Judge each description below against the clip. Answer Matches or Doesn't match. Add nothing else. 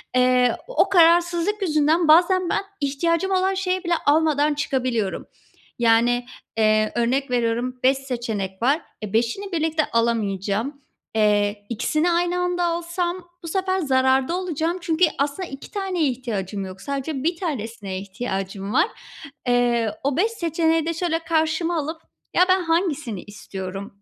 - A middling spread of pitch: Doesn't match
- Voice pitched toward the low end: Doesn't match